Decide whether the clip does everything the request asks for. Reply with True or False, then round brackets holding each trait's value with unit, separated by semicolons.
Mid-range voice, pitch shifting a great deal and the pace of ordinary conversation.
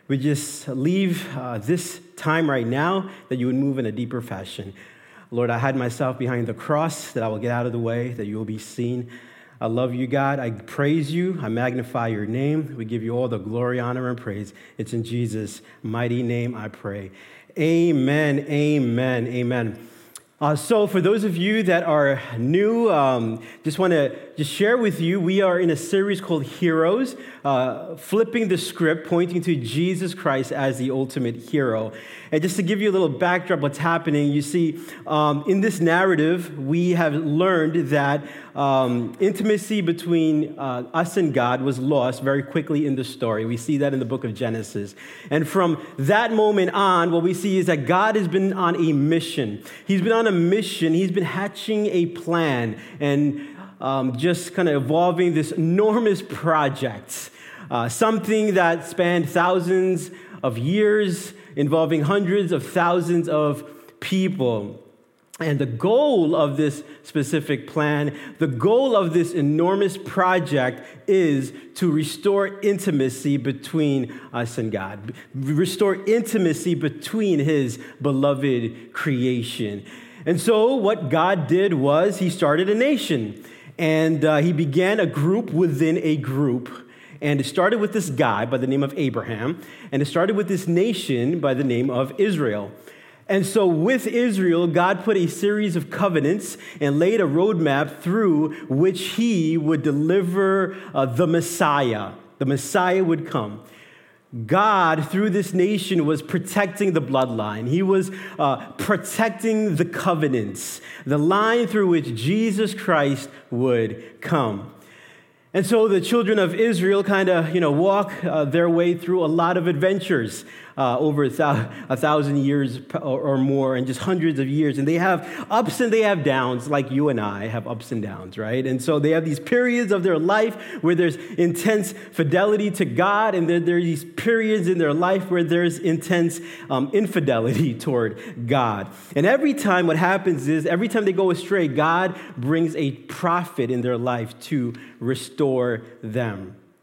True (160 Hz; 5.8 semitones; 165 wpm)